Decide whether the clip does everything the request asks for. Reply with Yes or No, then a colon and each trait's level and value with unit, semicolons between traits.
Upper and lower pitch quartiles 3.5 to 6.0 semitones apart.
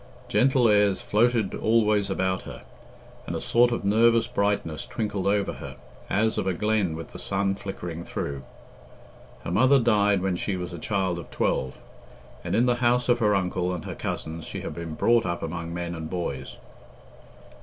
Yes: average, 4.3 semitones